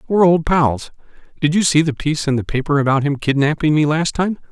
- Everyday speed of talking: No, fast, 225 wpm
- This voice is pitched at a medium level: Yes, medium, 150 Hz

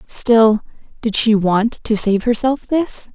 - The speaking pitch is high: Yes, high, 225 Hz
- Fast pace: No, average, 150 wpm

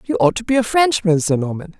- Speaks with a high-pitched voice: Yes, very high, 280 Hz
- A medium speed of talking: No, fast, 265 wpm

